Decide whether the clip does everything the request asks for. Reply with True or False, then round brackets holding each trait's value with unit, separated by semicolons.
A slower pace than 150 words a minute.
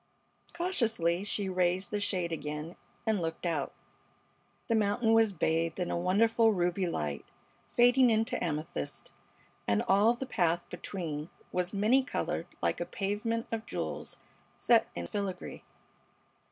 True (135 wpm)